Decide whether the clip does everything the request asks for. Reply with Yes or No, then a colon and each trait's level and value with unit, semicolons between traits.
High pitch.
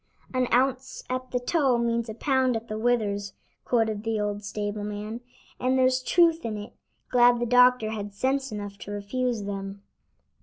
Yes: high, 235 Hz